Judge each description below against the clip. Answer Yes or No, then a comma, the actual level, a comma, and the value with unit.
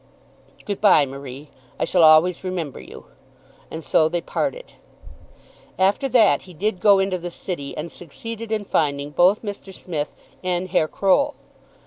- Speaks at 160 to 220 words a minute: No, average, 150 wpm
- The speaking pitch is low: No, medium, 180 Hz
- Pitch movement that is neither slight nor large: Yes, average, 4.4 semitones